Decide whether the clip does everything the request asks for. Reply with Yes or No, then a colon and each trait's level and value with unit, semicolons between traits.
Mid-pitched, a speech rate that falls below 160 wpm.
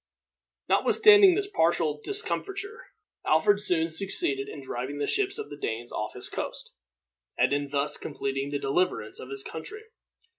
Yes: medium, 160 Hz; average, 150 wpm